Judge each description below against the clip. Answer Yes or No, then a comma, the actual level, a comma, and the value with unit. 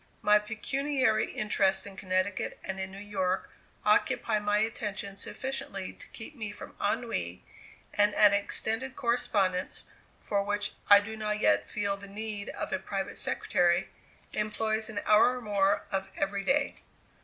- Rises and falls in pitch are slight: Yes, narrow, 2.0 semitones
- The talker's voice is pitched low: No, high, 205 Hz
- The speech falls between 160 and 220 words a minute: No, average, 150 wpm